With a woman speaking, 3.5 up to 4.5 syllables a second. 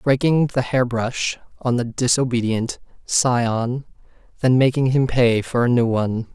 No: male; 4.2 syllables/s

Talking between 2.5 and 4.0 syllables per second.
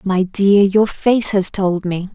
Yes: 3.5 syllables/s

